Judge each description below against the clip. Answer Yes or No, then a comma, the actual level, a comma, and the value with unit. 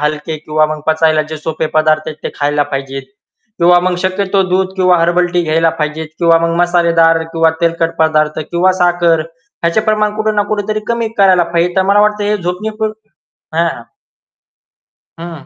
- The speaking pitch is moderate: Yes, medium, 170 Hz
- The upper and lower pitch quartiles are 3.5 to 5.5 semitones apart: No, average, 3.0 semitones